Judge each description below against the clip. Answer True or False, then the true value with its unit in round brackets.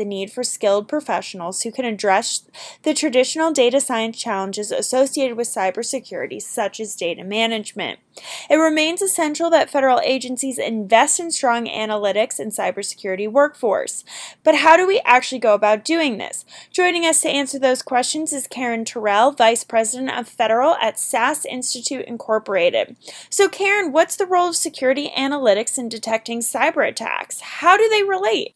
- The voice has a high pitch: True (255 Hz)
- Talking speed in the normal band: True (160 wpm)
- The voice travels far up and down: True (5.8 semitones)